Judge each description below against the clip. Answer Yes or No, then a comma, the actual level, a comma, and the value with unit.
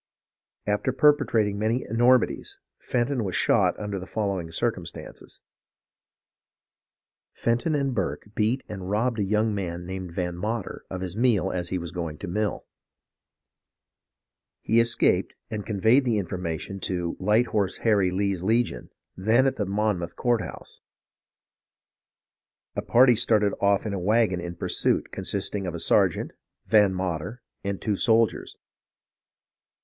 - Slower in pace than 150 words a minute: Yes, slow, 135 wpm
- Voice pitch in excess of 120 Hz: No, low, 105 Hz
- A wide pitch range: No, average, 3.7 semitones